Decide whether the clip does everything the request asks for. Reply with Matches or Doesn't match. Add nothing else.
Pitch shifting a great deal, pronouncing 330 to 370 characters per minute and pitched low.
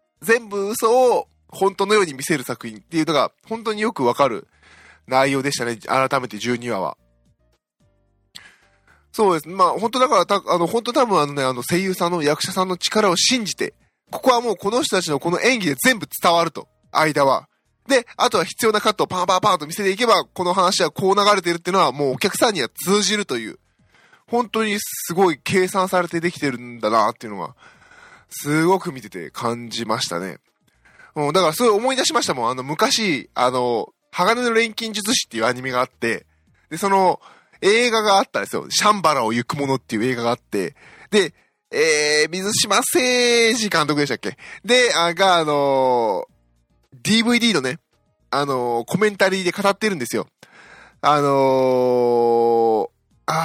Doesn't match